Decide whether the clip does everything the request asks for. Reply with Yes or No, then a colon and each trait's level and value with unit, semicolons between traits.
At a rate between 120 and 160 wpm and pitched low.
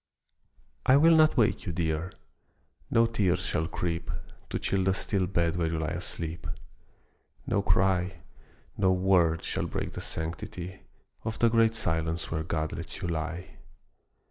Yes: average, 150 wpm; very low, 90 Hz